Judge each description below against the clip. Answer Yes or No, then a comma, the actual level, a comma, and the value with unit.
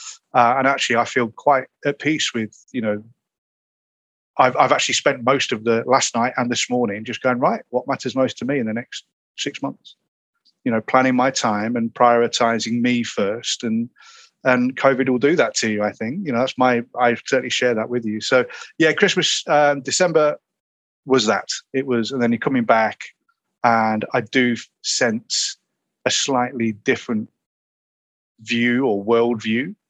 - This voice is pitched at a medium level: No, low, 125 Hz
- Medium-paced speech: Yes, average, 180 wpm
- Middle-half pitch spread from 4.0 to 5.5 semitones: No, narrow, 2.6 semitones